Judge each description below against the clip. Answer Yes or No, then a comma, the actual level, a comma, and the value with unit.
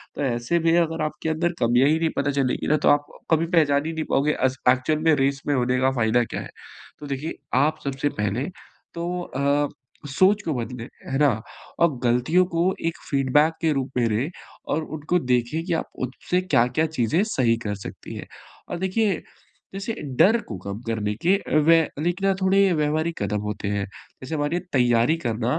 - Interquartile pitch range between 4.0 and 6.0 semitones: Yes, average, 4.8 semitones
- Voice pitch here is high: No, medium, 145 Hz